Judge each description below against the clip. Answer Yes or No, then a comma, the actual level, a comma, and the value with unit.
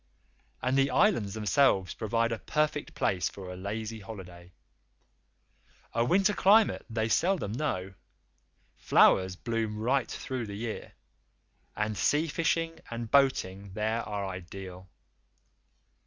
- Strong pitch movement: Yes, wide, 5.8 semitones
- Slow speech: Yes, slow, 120 wpm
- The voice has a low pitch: Yes, low, 110 Hz